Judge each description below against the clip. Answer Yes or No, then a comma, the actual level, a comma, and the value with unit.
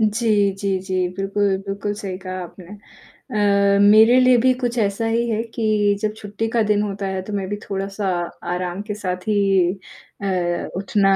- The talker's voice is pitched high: Yes, high, 200 Hz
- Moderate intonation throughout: No, narrow, 1.9 semitones